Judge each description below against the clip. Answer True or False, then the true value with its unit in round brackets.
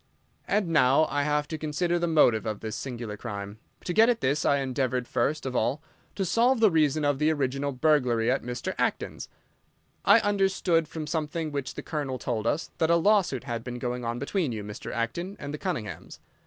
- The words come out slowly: False (200 wpm)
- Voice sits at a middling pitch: True (145 Hz)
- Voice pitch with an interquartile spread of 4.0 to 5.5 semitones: True (5.1 semitones)